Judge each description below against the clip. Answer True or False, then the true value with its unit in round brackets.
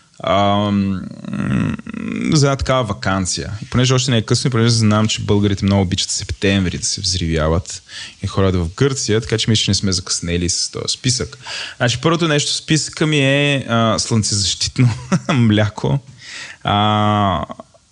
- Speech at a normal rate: True (150 wpm)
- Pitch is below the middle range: True (110 Hz)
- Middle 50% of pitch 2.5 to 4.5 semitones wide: False (4.9 semitones)